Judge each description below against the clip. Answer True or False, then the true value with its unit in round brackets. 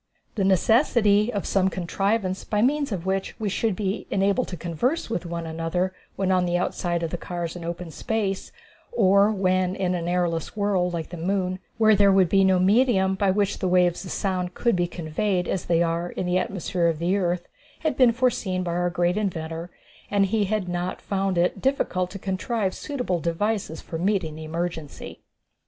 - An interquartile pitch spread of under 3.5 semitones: True (2.5 semitones)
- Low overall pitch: False (185 Hz)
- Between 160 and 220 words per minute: True (195 wpm)